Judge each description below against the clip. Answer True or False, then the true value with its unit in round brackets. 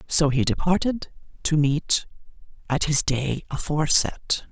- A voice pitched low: False (150 Hz)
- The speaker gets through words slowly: True (120 wpm)